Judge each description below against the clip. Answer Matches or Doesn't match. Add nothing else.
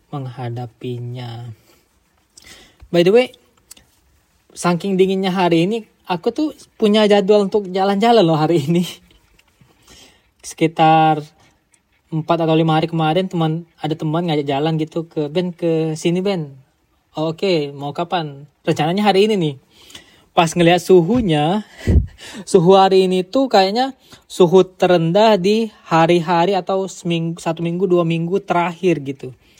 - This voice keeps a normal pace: Matches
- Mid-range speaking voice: Matches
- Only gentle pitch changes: Doesn't match